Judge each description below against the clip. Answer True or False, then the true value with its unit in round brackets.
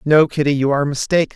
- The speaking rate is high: True (220 wpm)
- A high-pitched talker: False (145 Hz)